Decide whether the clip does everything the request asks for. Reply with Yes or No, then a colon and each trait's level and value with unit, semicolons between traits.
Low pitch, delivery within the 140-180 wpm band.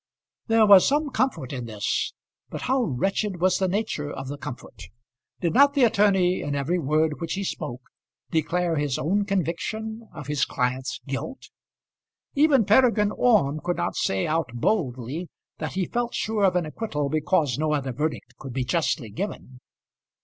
No: medium, 170 Hz; average, 165 wpm